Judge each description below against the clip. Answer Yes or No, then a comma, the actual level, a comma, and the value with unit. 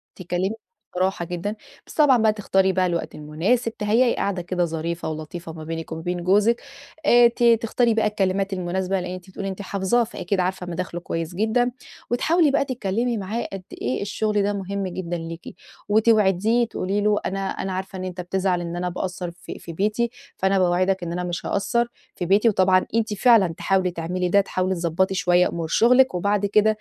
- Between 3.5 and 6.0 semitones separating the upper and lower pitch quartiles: No, average, 3.1 semitones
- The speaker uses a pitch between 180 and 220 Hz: Yes, high, 190 Hz